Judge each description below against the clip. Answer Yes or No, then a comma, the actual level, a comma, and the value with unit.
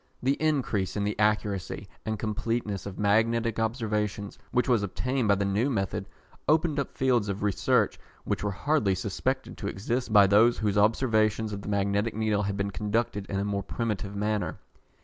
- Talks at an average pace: Yes, average, 175 wpm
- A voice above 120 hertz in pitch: No, low, 105 Hz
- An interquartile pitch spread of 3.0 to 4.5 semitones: No, narrow, 2.5 semitones